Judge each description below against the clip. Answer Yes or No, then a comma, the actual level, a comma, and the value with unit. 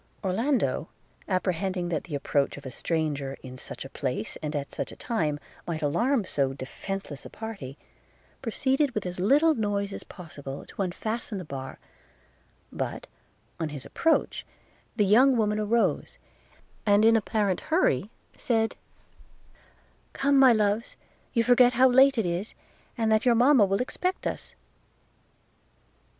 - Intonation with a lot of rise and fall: Yes, wide, 7.2 semitones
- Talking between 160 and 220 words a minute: No, average, 145 wpm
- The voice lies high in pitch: Yes, high, 205 Hz